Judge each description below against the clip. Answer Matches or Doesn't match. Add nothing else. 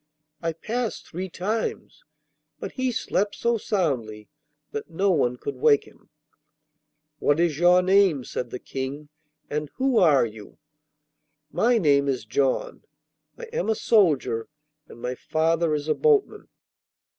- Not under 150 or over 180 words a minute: Doesn't match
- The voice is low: Doesn't match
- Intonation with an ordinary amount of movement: Doesn't match